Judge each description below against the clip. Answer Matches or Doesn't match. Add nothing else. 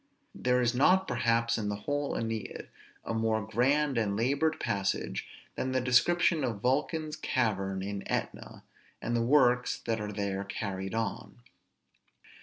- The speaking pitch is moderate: Doesn't match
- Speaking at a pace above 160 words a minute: Doesn't match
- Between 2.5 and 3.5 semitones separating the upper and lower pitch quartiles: Doesn't match